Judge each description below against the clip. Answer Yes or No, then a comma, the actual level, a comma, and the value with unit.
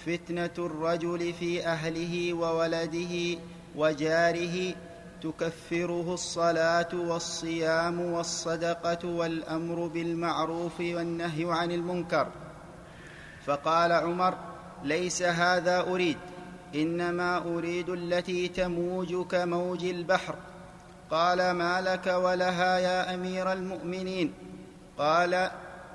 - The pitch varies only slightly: Yes, narrow, 1.2 semitones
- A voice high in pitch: No, medium, 175 Hz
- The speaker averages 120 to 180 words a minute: No, average, 80 wpm